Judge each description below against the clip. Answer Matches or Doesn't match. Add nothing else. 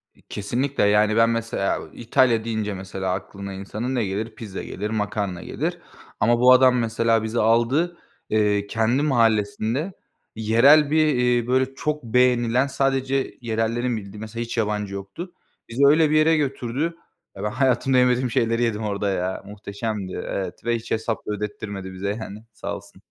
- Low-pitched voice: Matches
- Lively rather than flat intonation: Doesn't match